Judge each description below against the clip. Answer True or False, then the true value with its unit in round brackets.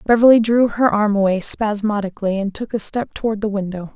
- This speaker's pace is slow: False (195 wpm)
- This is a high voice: True (210 Hz)